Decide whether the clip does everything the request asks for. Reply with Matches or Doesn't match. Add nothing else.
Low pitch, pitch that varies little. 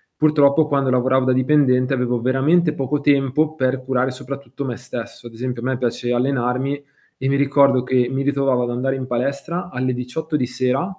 Matches